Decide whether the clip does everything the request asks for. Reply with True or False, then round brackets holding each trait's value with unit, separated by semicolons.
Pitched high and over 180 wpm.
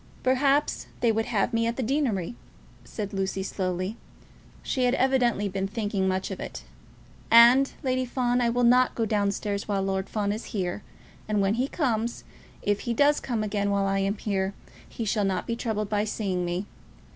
True (210 Hz; 190 wpm)